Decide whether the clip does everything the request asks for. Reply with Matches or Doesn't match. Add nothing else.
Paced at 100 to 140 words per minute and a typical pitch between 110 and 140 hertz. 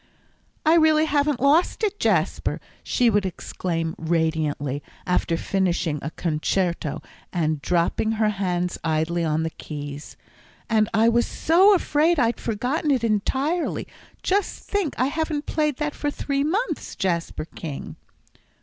Doesn't match